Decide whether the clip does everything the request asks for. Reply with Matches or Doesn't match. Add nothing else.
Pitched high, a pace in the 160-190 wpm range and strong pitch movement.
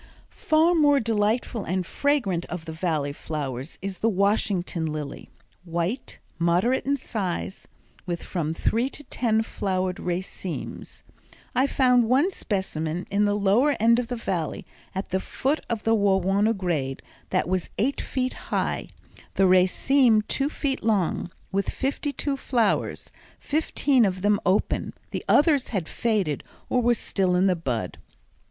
Doesn't match